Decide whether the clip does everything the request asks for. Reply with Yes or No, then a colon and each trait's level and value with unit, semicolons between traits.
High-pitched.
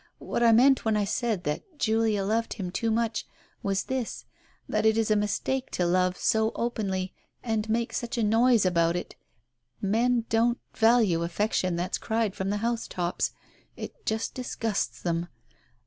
Yes: high, 220 Hz